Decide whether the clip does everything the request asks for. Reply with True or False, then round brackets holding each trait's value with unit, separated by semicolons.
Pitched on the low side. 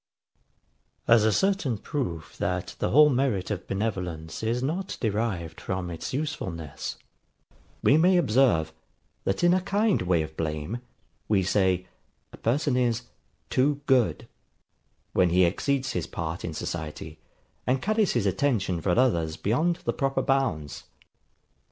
True (110 Hz)